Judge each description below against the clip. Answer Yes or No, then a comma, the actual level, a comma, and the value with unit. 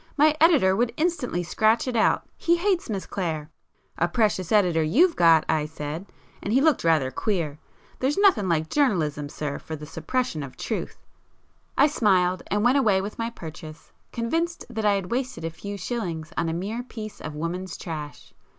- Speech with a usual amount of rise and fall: No, wide, 7.2 semitones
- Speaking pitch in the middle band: No, high, 195 Hz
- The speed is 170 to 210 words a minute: Yes, average, 180 wpm